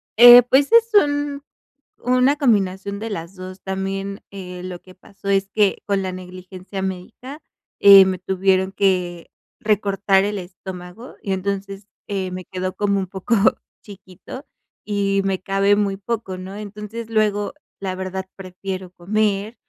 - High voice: Yes, high, 195 Hz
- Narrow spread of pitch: Yes, narrow, 2.1 semitones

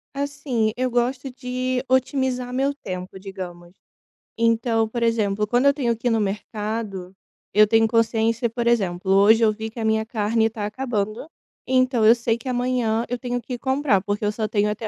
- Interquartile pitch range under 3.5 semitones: Yes, average, 2.9 semitones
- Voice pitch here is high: Yes, high, 230 Hz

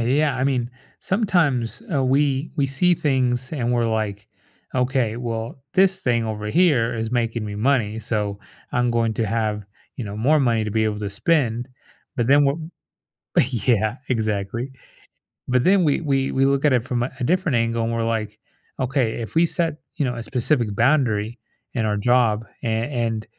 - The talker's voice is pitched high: No, low, 120 Hz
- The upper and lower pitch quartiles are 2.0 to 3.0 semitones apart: No, average, 3.5 semitones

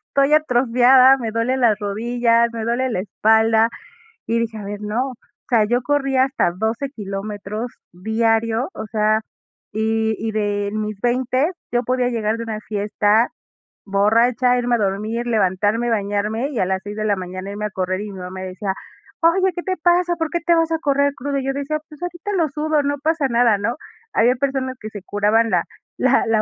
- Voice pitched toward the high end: Yes, high, 230 Hz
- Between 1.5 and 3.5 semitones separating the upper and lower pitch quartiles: No, average, 4.0 semitones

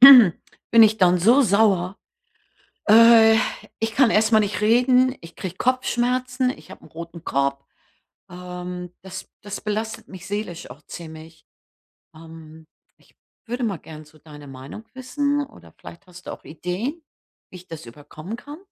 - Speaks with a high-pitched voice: Yes, high, 195 Hz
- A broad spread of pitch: Yes, wide, 5.9 semitones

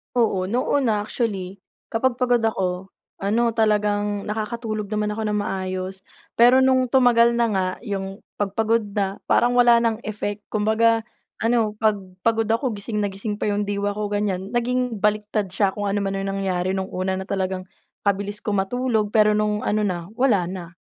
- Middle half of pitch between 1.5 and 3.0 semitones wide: Yes, average, 2.7 semitones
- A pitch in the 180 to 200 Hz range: No, high, 210 Hz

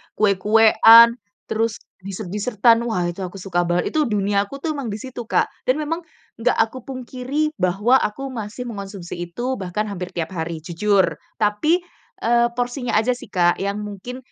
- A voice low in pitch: No, high, 215 Hz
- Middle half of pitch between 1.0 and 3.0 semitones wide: No, average, 4.2 semitones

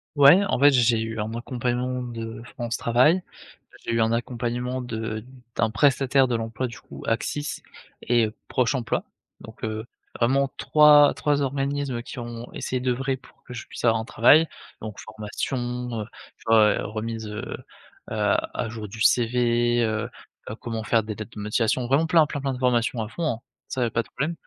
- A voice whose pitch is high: No, low, 120 Hz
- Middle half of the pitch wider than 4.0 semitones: No, narrow, 2.6 semitones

